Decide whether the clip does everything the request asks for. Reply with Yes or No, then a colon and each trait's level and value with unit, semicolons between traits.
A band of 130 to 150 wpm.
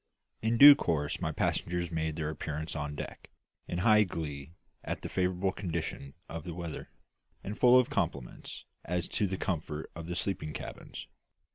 No: average, 165 wpm